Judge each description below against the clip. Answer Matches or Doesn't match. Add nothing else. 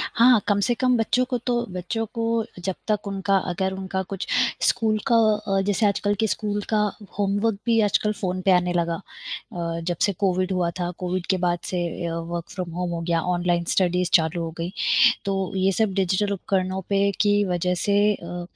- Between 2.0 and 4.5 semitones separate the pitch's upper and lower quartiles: Matches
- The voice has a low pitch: Doesn't match